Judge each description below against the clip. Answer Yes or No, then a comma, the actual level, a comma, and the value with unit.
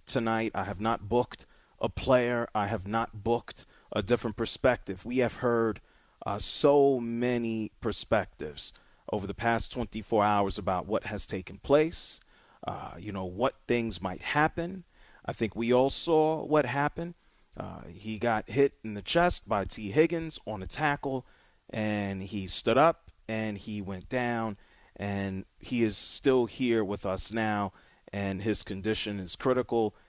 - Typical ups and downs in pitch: Yes, average, 3.8 semitones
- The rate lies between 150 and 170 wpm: Yes, average, 160 wpm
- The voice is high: No, low, 115 Hz